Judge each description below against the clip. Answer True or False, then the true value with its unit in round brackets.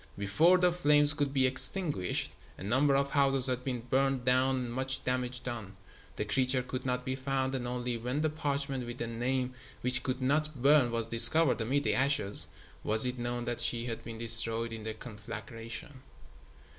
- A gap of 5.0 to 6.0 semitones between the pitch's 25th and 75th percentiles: False (2.6 semitones)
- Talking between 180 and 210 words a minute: True (185 wpm)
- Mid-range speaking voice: False (125 Hz)